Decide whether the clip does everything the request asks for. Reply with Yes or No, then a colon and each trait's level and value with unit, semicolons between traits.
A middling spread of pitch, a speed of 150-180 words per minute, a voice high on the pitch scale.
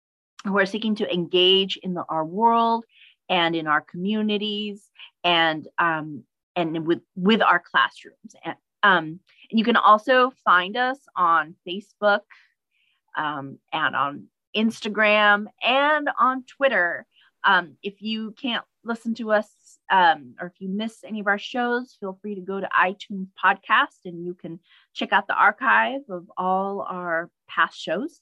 Yes: average, 3.9 semitones; average, 155 wpm; high, 205 Hz